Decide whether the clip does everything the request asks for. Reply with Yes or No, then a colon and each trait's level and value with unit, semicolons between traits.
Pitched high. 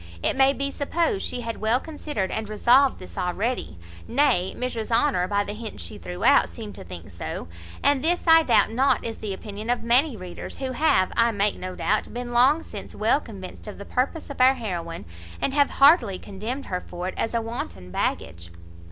Yes: high, 230 Hz